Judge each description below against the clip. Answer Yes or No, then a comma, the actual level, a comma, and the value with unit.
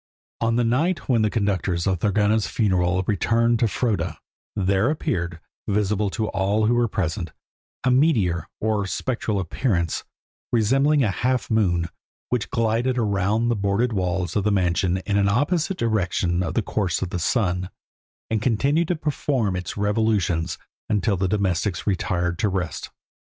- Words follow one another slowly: No, average, 155 wpm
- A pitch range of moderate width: Yes, average, 4.1 semitones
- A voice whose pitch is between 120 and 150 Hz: No, low, 105 Hz